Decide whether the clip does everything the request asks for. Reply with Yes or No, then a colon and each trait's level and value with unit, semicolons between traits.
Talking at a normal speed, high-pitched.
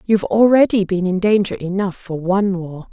Yes: average, 185 wpm; high, 195 Hz